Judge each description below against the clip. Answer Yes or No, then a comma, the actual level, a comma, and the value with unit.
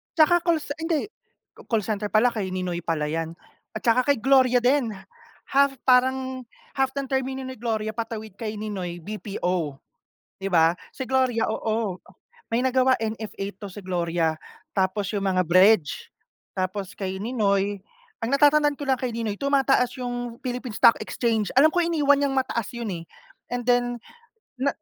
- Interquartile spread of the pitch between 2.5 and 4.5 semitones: No, average, 4.9 semitones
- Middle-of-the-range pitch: No, high, 230 Hz